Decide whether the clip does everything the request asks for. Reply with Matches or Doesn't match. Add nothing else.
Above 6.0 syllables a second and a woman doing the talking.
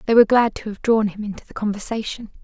Matches